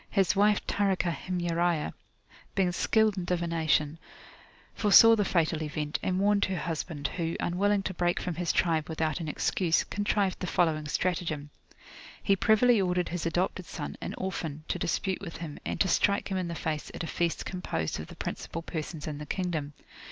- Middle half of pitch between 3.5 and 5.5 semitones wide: No, average, 3.1 semitones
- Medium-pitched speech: Yes, medium, 175 Hz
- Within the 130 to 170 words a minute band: No, average, 180 wpm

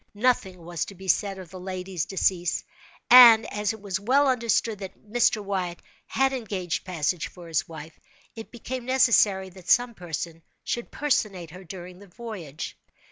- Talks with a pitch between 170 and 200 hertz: Yes, high, 190 Hz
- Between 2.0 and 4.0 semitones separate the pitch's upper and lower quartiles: No, average, 4.5 semitones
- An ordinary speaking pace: Yes, average, 165 wpm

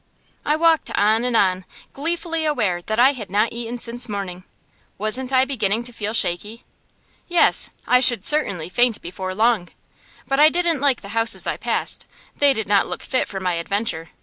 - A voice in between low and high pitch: No, high, 230 Hz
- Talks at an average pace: Yes, average, 180 wpm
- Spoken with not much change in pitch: No, average, 5.1 semitones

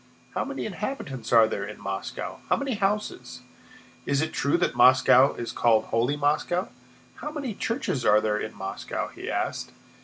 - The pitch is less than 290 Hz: Yes, medium, 140 Hz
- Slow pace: No, average, 165 wpm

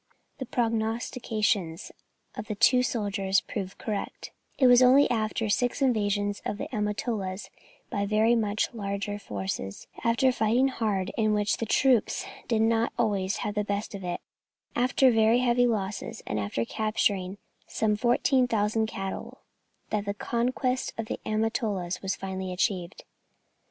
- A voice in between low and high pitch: No, high, 215 Hz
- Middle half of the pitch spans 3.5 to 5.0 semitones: No, average, 2.8 semitones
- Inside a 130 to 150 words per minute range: Yes, average, 140 wpm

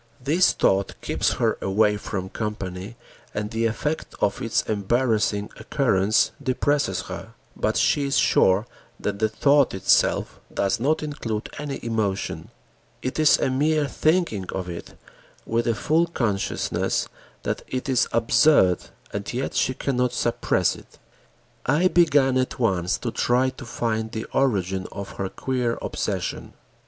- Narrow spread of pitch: No, average, 5.0 semitones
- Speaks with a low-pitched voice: Yes, low, 115 Hz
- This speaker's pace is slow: No, average, 145 wpm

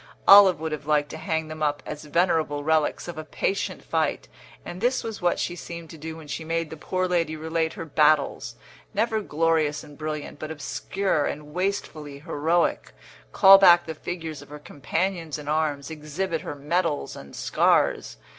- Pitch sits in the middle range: Yes, medium, 160 Hz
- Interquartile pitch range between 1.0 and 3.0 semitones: Yes, narrow, 2.6 semitones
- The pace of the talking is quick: No, average, 180 wpm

